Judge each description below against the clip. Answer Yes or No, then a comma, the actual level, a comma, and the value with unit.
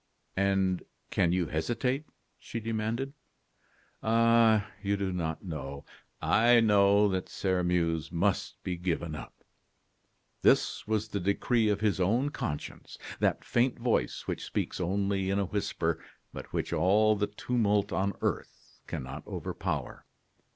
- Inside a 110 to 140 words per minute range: Yes, slow, 135 wpm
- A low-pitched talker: Yes, low, 100 Hz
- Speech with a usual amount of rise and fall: Yes, average, 3.6 semitones